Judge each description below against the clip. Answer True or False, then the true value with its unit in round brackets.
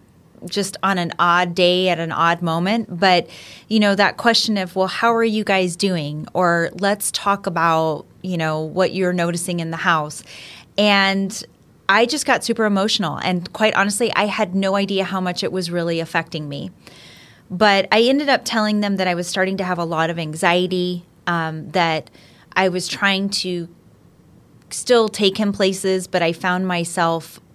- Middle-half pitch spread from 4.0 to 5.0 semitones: False (2.9 semitones)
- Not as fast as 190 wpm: True (180 wpm)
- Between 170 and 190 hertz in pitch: True (185 Hz)